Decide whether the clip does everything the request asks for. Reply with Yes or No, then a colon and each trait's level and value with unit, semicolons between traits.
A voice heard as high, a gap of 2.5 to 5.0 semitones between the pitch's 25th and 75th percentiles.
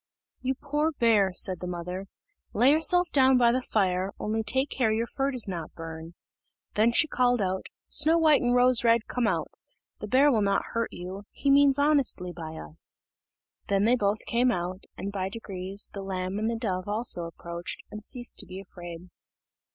No: high, 215 Hz; wide, 5.5 semitones